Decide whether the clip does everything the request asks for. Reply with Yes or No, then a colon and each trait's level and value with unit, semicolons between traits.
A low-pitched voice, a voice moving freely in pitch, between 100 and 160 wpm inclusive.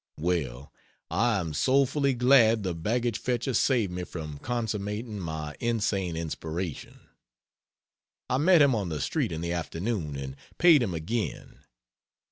Yes: low, 100 Hz; wide, 6.8 semitones; slow, 135 wpm